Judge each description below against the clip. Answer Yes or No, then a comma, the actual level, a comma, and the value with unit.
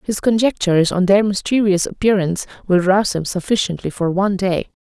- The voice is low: No, high, 190 Hz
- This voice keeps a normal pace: Yes, average, 160 wpm